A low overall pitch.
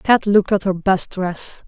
No: high, 190 Hz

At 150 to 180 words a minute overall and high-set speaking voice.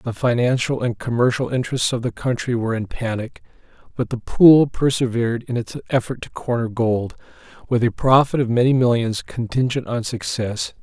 No: average, 165 wpm; low, 120 Hz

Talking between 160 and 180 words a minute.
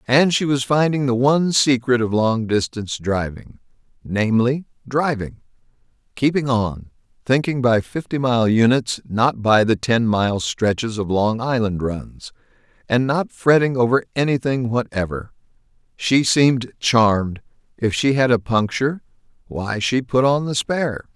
No: slow, 135 wpm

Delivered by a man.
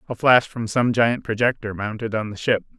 Yes: male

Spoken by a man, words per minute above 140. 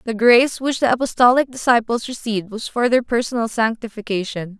No: female; average, 155 wpm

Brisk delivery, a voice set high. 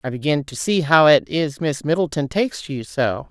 No: fast, 235 wpm; medium, 150 Hz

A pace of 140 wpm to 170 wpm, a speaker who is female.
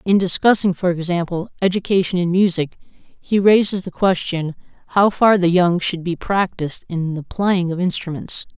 Yes: average, 160 wpm; female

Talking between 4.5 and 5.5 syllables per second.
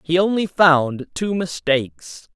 No: 3.7 syllables/s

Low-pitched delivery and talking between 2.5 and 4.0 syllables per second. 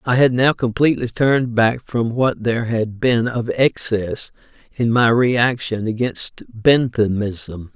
Yes: low, 115 Hz; 3.9 syllables/s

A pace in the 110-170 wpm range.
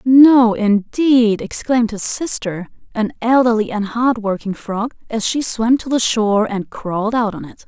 Yes: average, 165 wpm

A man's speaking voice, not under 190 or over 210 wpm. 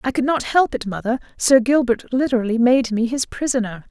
No: female; average, 200 wpm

